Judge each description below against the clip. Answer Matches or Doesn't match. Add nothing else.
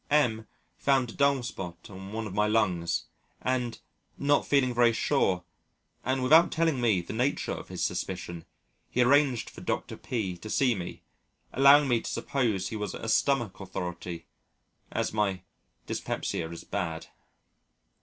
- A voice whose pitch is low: Matches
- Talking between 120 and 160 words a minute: Matches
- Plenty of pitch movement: Matches